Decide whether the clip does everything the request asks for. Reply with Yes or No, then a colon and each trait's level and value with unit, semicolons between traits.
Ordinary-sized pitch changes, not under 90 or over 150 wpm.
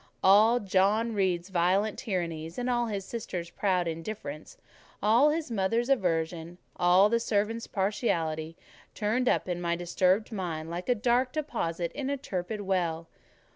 Yes: average, 4.8 semitones; average, 140 wpm